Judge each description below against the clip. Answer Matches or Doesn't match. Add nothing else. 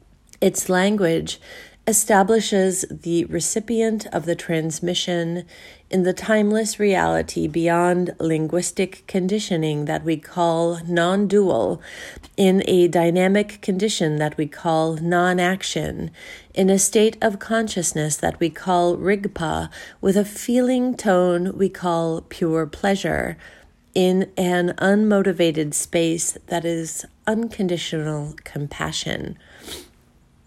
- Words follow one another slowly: Matches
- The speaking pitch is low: Doesn't match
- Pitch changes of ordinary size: Matches